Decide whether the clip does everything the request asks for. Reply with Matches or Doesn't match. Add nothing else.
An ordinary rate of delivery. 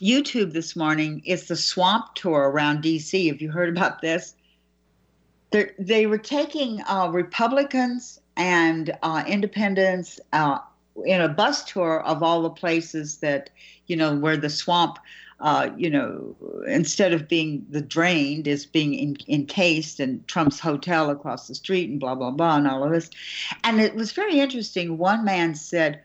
Matches